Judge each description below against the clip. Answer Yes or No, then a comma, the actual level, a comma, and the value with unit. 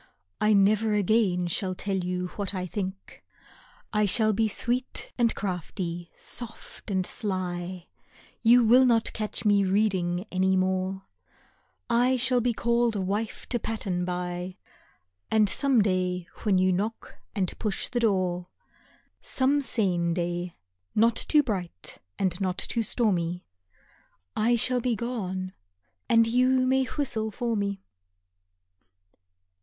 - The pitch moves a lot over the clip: No, average, 4.0 semitones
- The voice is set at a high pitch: Yes, high, 200 Hz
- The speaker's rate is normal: No, slow, 130 wpm